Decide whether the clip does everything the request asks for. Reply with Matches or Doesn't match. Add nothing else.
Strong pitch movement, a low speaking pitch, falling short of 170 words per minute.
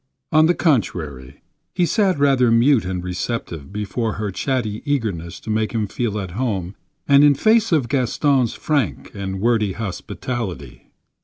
Matches